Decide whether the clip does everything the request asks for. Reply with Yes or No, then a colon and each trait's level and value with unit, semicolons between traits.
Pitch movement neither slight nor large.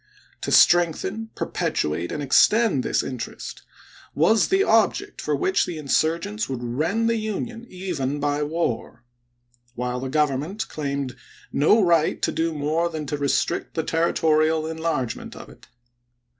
Yes: average, 4.2 semitones